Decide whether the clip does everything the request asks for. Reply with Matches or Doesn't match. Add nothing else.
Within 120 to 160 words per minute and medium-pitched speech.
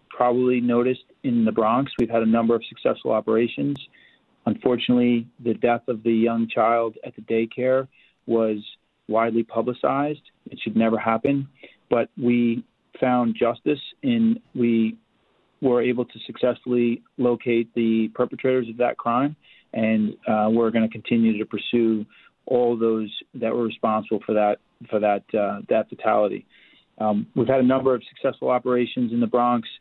Doesn't match